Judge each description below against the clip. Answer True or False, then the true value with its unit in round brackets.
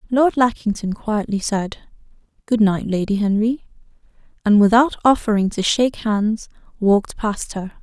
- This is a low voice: False (215 Hz)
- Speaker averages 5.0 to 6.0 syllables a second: False (4.6 syllables/s)